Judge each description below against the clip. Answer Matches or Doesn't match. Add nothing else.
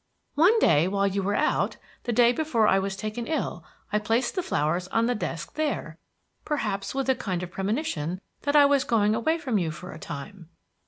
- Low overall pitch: Doesn't match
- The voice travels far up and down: Matches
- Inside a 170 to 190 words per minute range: Doesn't match